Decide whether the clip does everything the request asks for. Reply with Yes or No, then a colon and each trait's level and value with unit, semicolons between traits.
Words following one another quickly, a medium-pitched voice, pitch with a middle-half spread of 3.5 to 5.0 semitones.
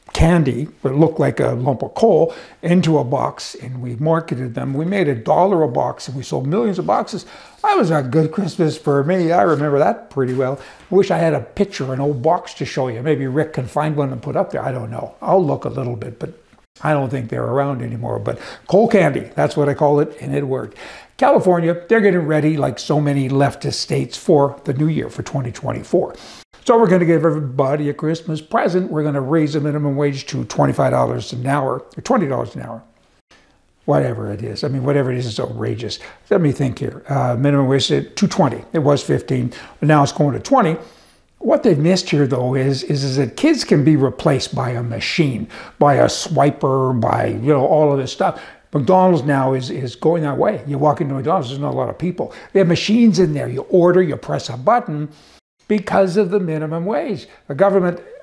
Yes: fast, 220 wpm; medium, 150 Hz; average, 3.9 semitones